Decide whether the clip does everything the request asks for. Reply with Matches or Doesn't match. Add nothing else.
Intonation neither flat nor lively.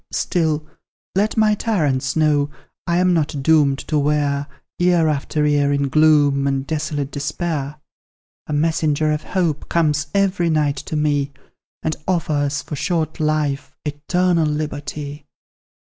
Doesn't match